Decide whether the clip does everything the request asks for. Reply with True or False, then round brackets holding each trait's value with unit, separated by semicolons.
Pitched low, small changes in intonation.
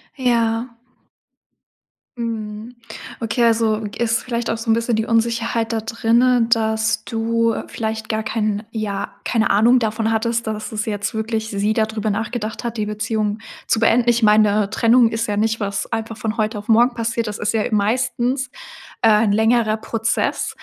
False (225 Hz; 1.3 semitones)